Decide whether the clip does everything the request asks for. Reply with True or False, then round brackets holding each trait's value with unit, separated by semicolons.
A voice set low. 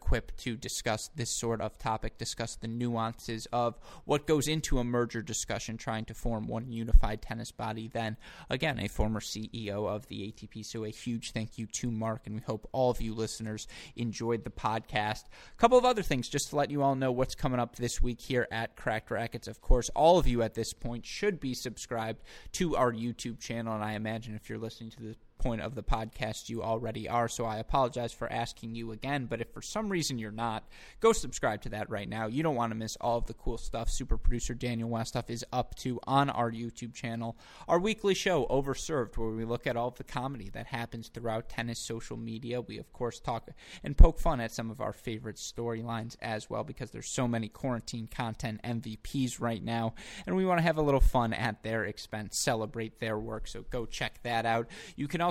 True (115 Hz)